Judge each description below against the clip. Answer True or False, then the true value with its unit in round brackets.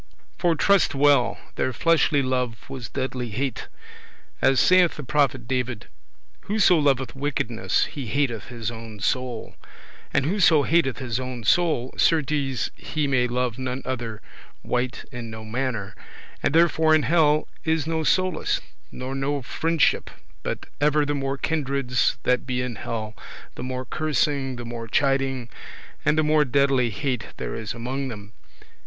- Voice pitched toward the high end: False (135 Hz)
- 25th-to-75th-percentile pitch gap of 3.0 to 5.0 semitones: True (3.4 semitones)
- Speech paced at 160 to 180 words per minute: False (150 wpm)